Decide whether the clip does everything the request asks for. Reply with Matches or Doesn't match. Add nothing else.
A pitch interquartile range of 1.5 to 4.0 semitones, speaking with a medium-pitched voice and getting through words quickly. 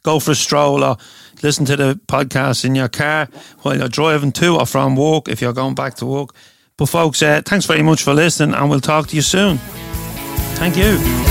Matches